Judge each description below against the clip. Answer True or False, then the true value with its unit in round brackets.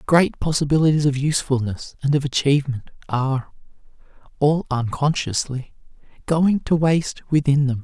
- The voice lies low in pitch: False (145 Hz)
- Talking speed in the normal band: False (115 wpm)